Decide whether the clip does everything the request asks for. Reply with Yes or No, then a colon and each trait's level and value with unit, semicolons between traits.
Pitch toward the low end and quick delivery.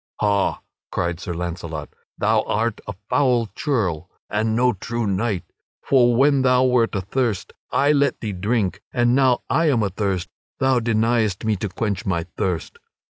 No: low, 110 Hz; average, 160 wpm